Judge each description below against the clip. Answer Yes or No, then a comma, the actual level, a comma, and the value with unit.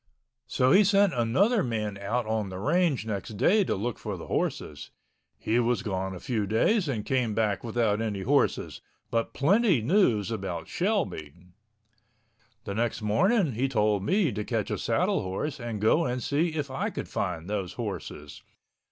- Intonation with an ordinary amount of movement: No, wide, 6.3 semitones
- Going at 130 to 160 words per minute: No, average, 170 wpm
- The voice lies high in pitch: No, low, 115 Hz